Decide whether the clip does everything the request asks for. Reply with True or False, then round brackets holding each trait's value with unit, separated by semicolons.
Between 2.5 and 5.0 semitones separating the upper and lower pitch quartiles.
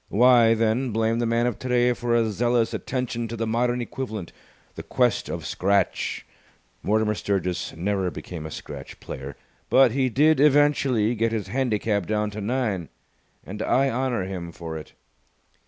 True (3.5 semitones)